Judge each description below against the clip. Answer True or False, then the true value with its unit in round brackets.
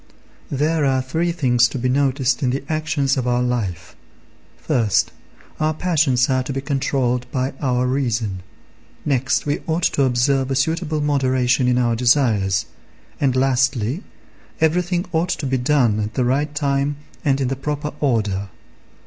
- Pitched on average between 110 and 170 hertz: True (135 Hz)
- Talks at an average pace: True (155 wpm)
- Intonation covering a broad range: False (3.0 semitones)